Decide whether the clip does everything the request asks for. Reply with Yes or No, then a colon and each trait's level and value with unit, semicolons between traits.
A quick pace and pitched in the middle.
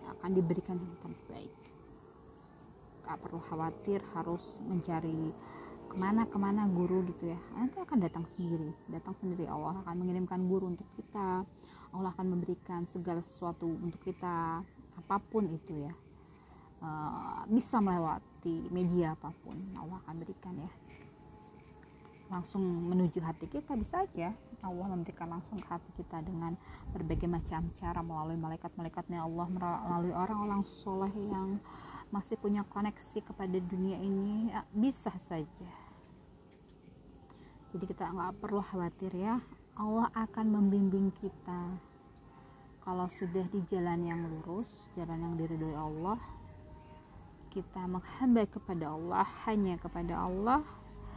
No: average, 120 wpm; medium, 180 Hz